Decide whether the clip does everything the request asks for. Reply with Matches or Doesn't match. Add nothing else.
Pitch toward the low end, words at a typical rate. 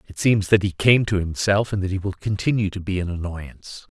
Doesn't match